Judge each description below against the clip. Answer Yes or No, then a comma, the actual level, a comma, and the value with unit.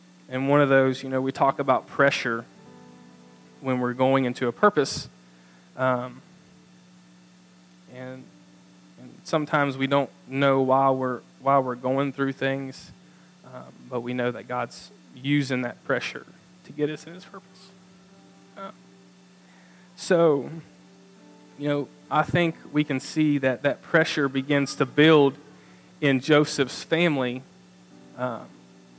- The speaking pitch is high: No, low, 135 Hz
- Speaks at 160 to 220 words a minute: No, slow, 135 wpm